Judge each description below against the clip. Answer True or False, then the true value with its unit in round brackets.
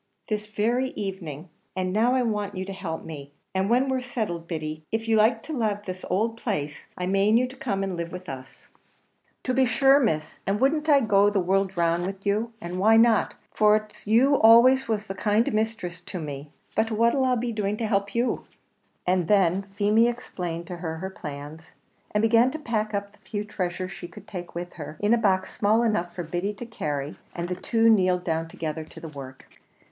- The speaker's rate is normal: False (215 wpm)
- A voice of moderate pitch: False (200 Hz)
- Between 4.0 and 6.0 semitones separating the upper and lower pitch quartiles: True (4.4 semitones)